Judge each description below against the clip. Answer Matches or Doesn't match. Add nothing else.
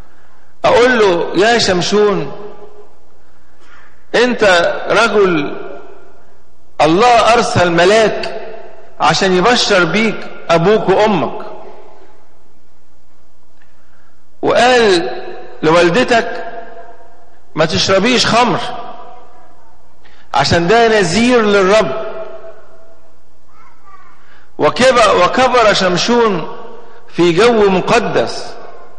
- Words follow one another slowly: Matches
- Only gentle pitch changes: Doesn't match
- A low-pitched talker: Doesn't match